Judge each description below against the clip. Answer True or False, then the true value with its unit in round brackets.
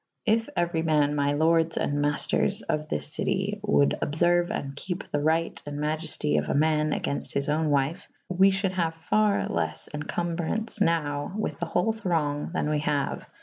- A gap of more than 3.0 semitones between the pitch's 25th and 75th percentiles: True (3.4 semitones)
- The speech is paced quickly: False (180 wpm)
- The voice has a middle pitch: True (160 Hz)